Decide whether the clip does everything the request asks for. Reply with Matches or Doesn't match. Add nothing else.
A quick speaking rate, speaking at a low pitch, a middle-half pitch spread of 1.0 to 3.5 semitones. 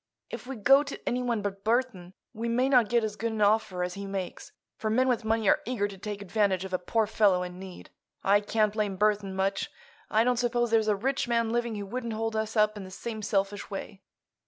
Doesn't match